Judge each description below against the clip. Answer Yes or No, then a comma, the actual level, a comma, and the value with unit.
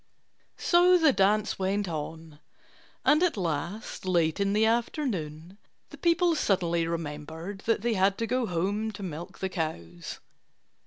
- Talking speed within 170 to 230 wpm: No, average, 145 wpm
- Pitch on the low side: No, high, 195 Hz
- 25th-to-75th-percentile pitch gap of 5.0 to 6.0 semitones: Yes, average, 5.3 semitones